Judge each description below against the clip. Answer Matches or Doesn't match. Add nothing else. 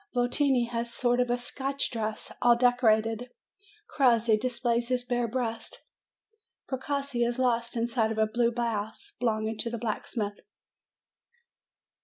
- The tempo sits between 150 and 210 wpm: Doesn't match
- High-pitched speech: Matches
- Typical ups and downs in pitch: Doesn't match